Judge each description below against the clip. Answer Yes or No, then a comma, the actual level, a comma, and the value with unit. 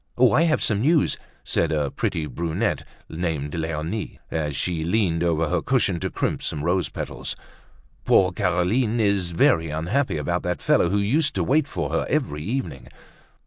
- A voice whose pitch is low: Yes, very low, 90 Hz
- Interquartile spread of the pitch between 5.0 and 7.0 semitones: Yes, wide, 5.6 semitones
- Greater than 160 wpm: Yes, average, 170 wpm